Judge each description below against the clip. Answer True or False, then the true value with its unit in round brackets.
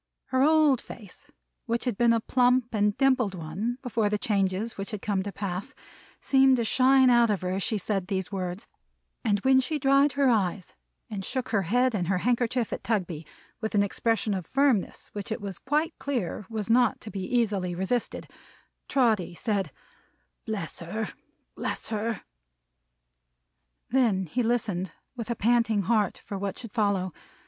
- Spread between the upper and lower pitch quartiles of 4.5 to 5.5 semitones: False (4.0 semitones)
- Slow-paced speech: False (170 wpm)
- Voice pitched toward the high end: True (220 Hz)